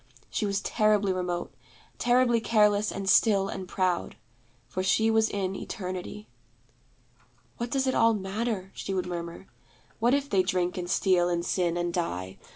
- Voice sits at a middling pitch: No, high, 195 Hz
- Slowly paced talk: No, average, 160 wpm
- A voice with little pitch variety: No, average, 3.4 semitones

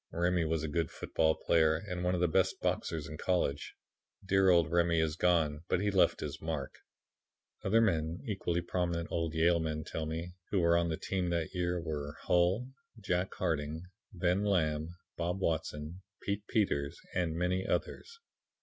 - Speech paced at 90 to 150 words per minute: No, average, 170 wpm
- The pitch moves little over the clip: Yes, narrow, 2.3 semitones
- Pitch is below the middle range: Yes, very low, 85 Hz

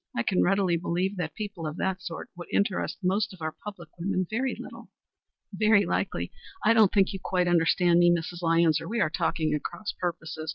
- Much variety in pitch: No, average, 3.0 semitones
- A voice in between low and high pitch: Yes, medium, 180 Hz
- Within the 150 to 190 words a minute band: No, fast, 205 wpm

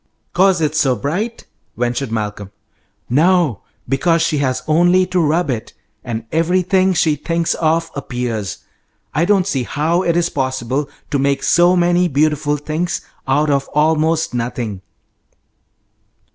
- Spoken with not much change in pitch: No, average, 4.6 semitones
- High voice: No, medium, 155 Hz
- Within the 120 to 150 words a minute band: Yes, slow, 135 wpm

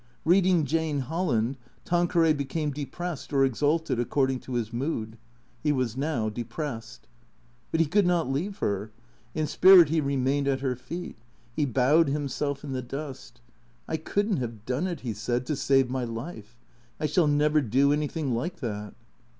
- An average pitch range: Yes, average, 4.5 semitones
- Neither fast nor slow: Yes, average, 170 wpm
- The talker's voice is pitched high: No, medium, 140 Hz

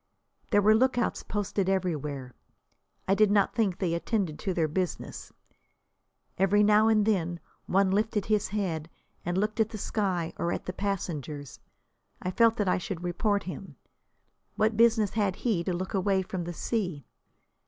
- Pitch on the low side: No, high, 195 Hz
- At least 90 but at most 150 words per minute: No, average, 165 wpm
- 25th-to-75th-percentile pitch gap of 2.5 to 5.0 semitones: Yes, average, 3.3 semitones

